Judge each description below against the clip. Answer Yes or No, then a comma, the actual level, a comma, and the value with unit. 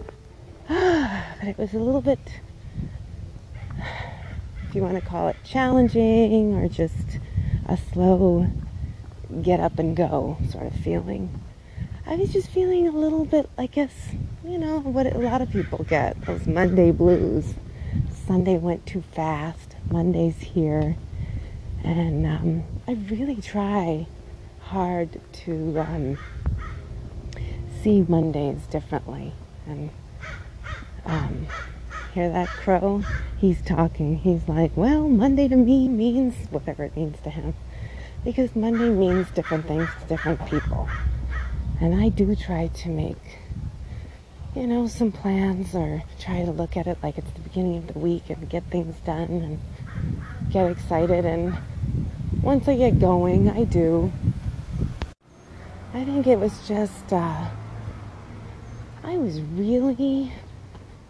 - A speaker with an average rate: No, slow, 130 wpm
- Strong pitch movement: Yes, wide, 6.4 semitones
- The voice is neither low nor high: Yes, medium, 175 Hz